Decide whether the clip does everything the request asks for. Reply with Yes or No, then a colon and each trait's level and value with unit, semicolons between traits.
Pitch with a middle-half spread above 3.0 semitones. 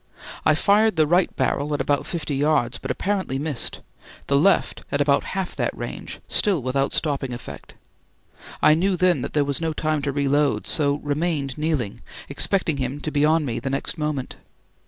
No: average, 2.7 semitones